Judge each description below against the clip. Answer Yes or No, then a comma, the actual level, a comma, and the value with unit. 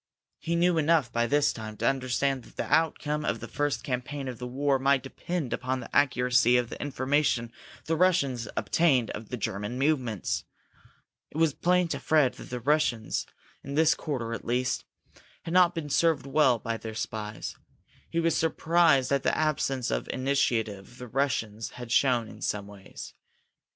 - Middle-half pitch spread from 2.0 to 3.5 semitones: No, average, 4.1 semitones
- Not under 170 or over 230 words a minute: Yes, average, 175 wpm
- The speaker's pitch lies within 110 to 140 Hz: Yes, low, 135 Hz